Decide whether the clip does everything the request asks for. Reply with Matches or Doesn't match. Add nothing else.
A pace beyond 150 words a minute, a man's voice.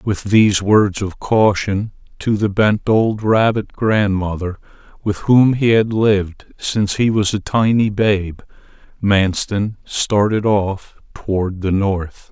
Doesn't match